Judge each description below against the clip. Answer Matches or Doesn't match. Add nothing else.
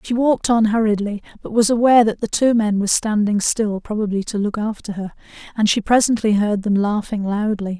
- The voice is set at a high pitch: Matches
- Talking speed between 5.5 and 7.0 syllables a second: Matches